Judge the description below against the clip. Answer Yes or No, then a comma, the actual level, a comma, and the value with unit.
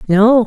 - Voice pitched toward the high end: Yes, high, 220 Hz